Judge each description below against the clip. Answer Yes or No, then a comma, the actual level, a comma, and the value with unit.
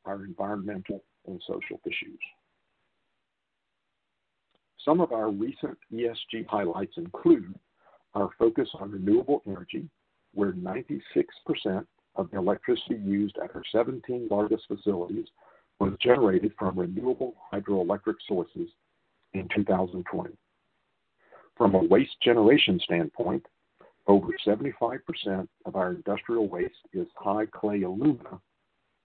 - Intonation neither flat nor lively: No, wide, 8.9 semitones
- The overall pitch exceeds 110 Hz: No, low, 105 Hz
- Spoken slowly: Yes, slow, 105 wpm